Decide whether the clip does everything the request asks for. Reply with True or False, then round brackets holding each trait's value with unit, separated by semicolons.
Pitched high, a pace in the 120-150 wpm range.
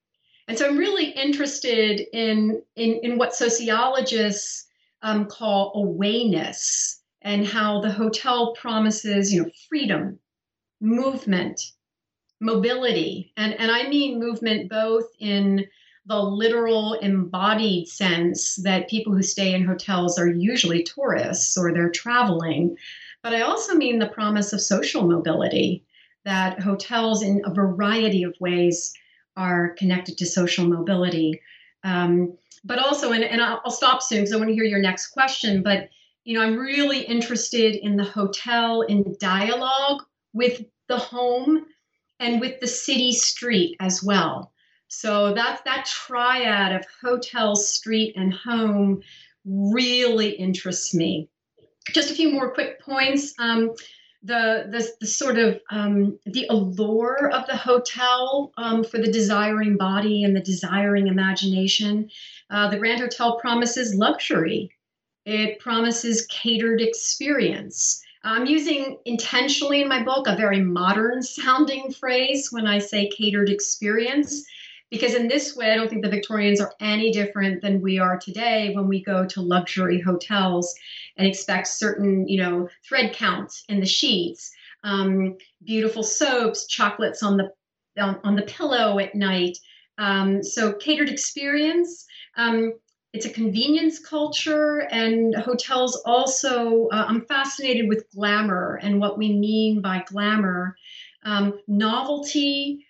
True (220 Hz; 140 wpm)